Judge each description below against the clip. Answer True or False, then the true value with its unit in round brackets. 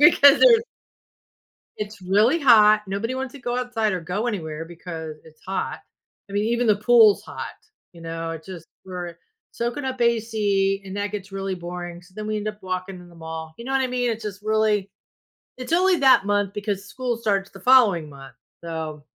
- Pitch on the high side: True (205 Hz)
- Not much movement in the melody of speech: False (4.7 semitones)